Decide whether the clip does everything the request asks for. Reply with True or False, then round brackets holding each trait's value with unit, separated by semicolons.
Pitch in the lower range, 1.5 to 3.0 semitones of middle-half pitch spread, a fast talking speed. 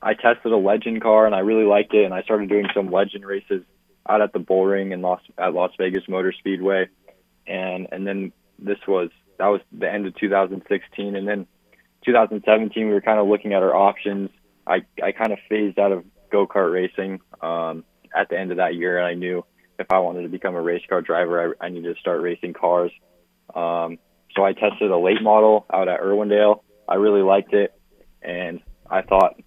True (95 Hz; 2.5 semitones; 210 wpm)